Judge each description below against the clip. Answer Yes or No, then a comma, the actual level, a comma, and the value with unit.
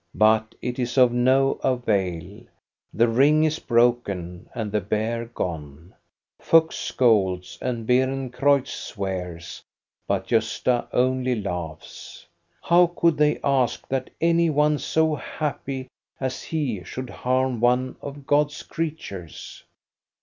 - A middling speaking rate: No, slow, 120 wpm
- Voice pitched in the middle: No, low, 125 Hz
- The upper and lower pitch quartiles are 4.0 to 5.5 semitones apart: Yes, average, 4.9 semitones